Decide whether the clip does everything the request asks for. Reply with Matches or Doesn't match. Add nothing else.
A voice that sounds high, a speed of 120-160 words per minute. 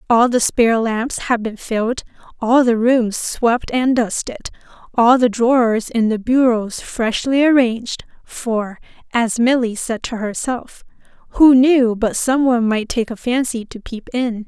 Matches